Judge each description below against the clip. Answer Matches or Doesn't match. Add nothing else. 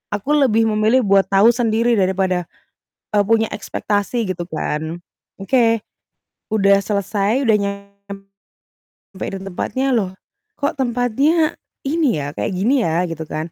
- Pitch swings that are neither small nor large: Matches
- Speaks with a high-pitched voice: Matches